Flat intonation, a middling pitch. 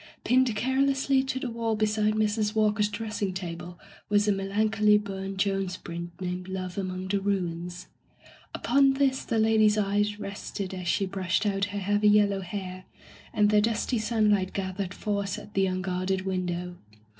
No: narrow, 2.3 semitones; high, 200 Hz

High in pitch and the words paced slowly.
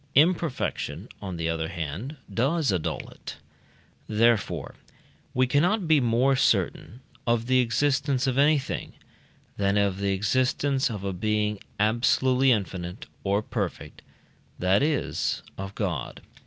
No: low, 115 Hz; slow, 125 wpm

